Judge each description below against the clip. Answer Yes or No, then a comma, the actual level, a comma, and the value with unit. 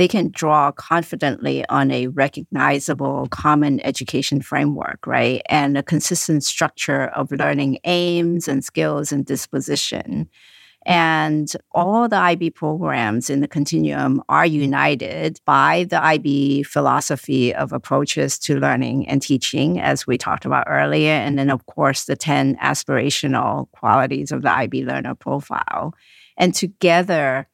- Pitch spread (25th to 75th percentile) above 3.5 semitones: No, average, 3.0 semitones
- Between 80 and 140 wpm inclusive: Yes, slow, 135 wpm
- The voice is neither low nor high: Yes, medium, 145 Hz